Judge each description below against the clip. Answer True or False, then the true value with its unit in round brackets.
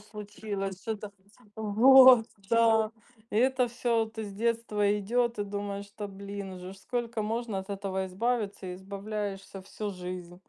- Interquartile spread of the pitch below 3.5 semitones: True (2.7 semitones)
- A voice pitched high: True (205 Hz)